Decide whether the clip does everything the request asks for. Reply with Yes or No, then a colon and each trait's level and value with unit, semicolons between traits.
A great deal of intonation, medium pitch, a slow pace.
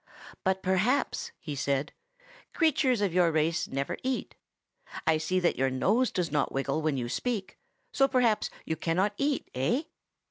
No: wide, 8.3 semitones; medium, 180 Hz; average, 155 wpm